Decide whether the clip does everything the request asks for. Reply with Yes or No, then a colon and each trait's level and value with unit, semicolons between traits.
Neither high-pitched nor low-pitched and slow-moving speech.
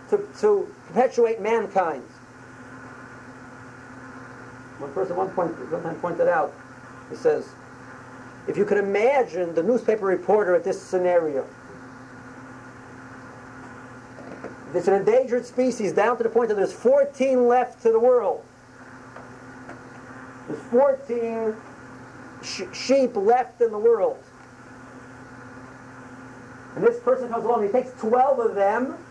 Yes: medium, 180 Hz; slow, 120 wpm